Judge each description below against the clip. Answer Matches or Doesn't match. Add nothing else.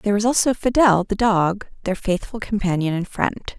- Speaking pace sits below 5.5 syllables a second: Matches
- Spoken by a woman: Matches